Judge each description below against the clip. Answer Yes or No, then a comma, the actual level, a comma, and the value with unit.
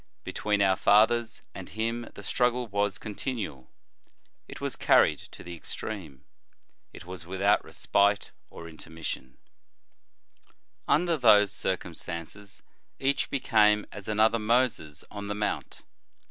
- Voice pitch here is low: Yes, low, 105 Hz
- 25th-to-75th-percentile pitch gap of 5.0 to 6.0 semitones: No, average, 3.5 semitones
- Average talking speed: No, slow, 120 wpm